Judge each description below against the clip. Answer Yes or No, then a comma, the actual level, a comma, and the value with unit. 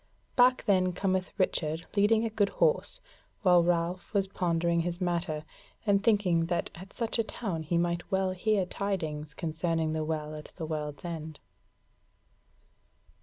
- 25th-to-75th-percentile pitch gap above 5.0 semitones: No, average, 3.5 semitones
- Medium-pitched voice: Yes, medium, 175 Hz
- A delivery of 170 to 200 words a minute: No, average, 150 wpm